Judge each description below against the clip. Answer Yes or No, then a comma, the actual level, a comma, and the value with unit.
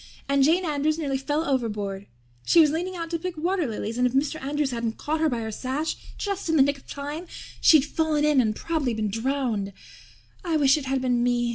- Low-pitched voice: No, very high, 280 Hz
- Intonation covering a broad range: No, average, 4.5 semitones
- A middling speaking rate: No, fast, 225 wpm